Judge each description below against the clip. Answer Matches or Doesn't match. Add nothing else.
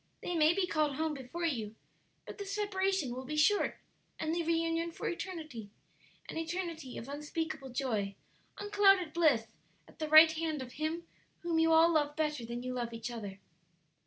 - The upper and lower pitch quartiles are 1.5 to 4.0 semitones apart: Doesn't match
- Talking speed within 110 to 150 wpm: Doesn't match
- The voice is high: Matches